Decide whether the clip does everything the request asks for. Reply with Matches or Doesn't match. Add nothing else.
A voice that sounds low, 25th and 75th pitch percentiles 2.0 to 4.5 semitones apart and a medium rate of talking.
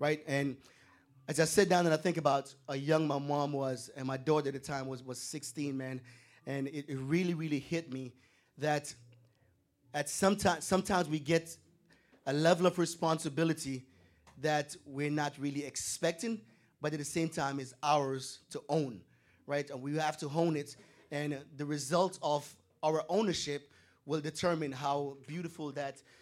Doesn't match